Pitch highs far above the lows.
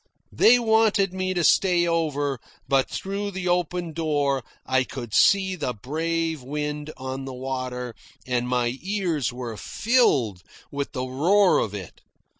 Yes: wide, 5.9 semitones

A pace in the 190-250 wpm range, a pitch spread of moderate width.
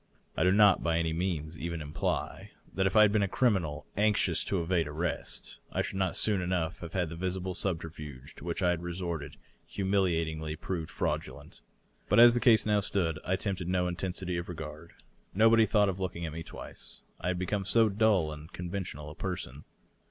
Yes: average, 195 wpm; average, 3.0 semitones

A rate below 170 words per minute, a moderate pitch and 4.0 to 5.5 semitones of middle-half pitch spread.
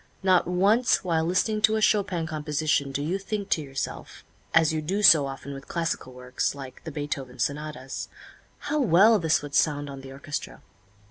No: average, 180 wpm; medium, 155 Hz; average, 5.0 semitones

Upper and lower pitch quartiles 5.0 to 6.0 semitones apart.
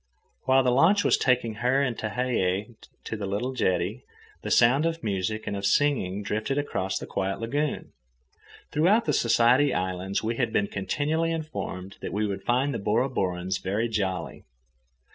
Yes: wide, 5.6 semitones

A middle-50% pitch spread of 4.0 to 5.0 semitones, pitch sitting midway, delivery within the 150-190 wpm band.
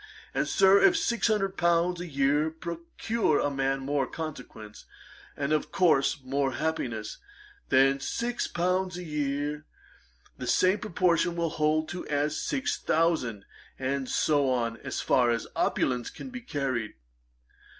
No: average, 4.7 semitones; medium, 150 Hz; average, 140 wpm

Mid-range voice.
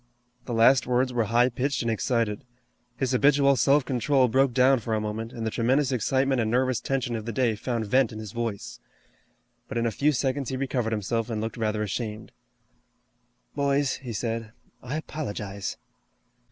No: low, 120 Hz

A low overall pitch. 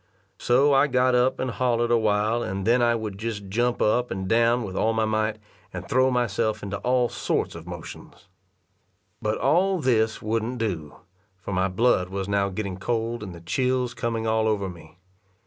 Yes: low, 110 Hz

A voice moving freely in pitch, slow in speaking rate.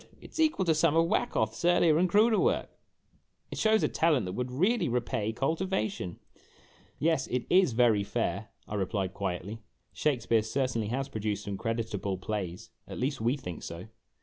No: wide, 7.9 semitones; average, 175 wpm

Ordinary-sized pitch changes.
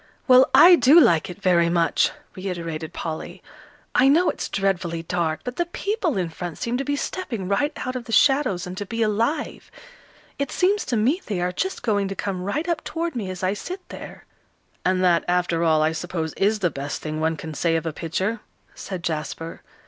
No: wide, 7.2 semitones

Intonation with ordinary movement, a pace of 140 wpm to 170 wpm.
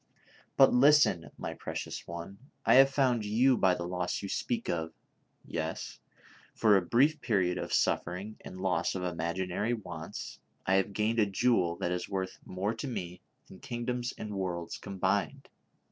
Yes: average, 4.9 semitones; average, 165 wpm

